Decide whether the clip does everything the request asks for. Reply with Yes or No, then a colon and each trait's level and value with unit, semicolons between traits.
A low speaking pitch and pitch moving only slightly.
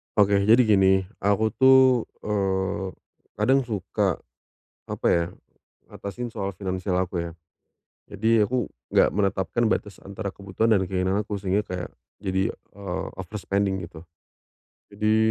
Yes: low, 100 Hz; narrow, 2.3 semitones